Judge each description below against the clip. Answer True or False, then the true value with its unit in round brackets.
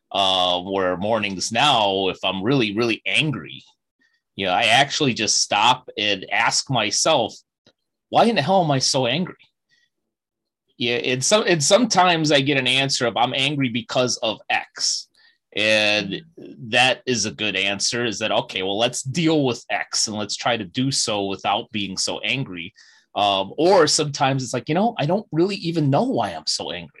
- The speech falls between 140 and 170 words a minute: False (180 wpm)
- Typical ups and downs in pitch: False (6.3 semitones)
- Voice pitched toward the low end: True (125 Hz)